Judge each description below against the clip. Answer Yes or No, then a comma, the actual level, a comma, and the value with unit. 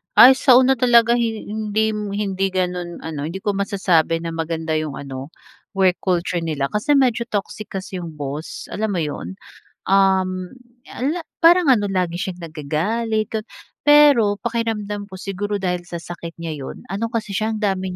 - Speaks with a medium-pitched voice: No, high, 195 Hz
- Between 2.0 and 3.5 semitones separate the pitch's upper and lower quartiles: No, average, 4.3 semitones